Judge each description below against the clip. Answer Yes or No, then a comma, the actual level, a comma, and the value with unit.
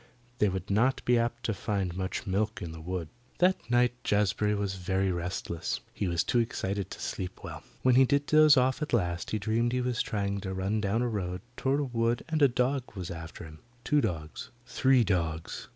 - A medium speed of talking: No, fast, 210 wpm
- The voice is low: Yes, low, 105 Hz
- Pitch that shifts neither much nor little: Yes, average, 5.0 semitones